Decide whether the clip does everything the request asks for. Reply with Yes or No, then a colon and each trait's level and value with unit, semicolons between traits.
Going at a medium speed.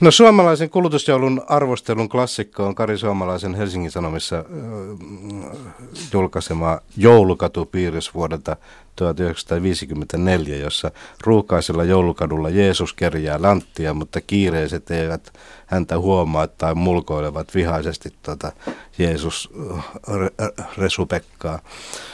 No: slow, 85 wpm